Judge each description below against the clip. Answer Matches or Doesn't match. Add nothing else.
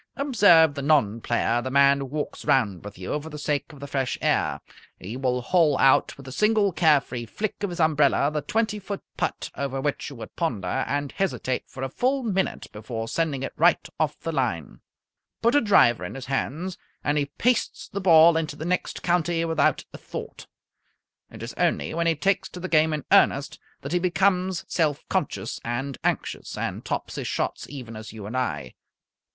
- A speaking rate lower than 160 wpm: Doesn't match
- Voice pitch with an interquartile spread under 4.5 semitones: Doesn't match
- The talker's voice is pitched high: Doesn't match